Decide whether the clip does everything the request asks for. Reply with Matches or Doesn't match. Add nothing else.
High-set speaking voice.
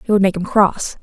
Matches